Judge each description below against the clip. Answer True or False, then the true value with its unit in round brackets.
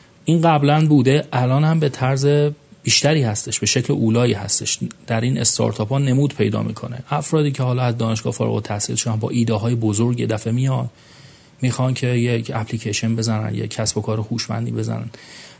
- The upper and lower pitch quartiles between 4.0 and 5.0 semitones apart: False (3.6 semitones)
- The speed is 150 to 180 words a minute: True (175 wpm)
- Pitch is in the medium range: False (120 Hz)